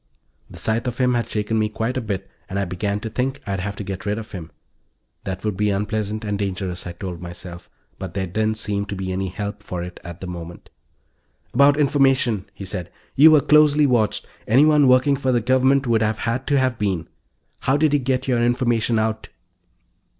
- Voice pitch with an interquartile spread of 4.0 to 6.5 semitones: Yes, average, 4.8 semitones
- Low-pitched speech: Yes, low, 110 Hz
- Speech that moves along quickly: Yes, fast, 210 wpm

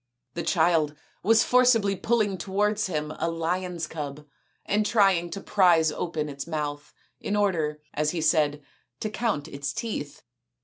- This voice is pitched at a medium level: Yes, medium, 170 Hz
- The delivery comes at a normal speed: Yes, average, 150 wpm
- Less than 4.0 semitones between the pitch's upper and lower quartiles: No, average, 5.1 semitones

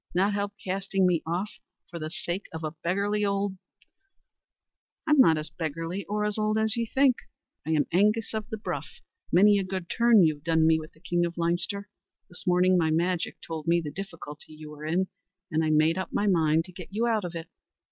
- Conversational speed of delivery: No, fast, 215 wpm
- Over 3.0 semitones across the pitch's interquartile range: Yes, average, 3.9 semitones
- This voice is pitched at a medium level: Yes, medium, 180 Hz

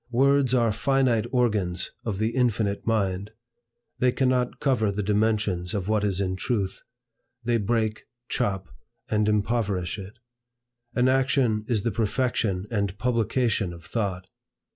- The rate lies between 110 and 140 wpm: Yes, slow, 135 wpm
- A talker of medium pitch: No, low, 110 Hz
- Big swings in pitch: No, average, 3.5 semitones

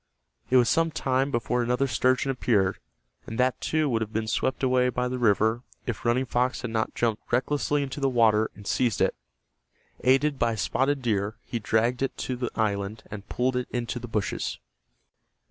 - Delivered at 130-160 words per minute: No, average, 185 wpm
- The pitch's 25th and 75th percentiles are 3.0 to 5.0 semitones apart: No, narrow, 2.6 semitones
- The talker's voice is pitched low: Yes, low, 125 Hz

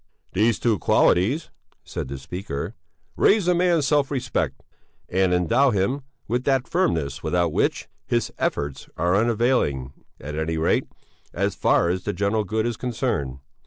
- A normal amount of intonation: No, wide, 7.6 semitones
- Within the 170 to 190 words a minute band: No, average, 150 wpm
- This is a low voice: Yes, low, 105 Hz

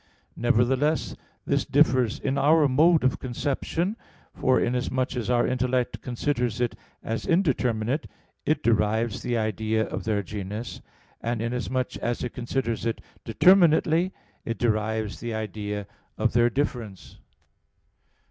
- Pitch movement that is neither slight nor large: Yes, average, 3.1 semitones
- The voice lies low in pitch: Yes, low, 120 Hz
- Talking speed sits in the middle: No, slow, 125 wpm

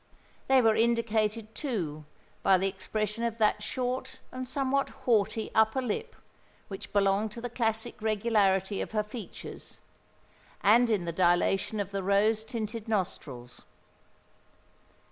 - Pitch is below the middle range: No, high, 215 Hz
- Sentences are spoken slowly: Yes, slow, 130 wpm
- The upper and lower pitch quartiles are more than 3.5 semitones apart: No, average, 2.9 semitones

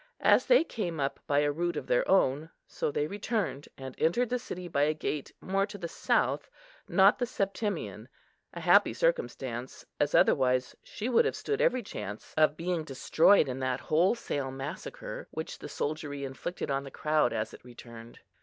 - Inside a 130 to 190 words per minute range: Yes, average, 180 wpm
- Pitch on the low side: No, medium, 155 Hz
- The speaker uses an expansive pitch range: Yes, wide, 6.6 semitones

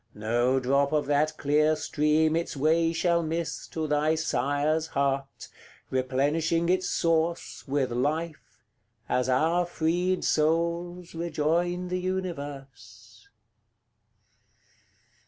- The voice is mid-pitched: Yes, medium, 155 Hz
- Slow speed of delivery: Yes, slow, 100 wpm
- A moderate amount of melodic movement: Yes, average, 3.1 semitones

